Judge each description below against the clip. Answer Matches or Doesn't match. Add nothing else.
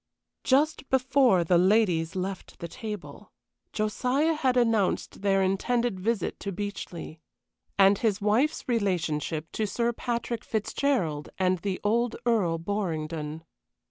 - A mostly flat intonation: Doesn't match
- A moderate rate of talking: Doesn't match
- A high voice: Matches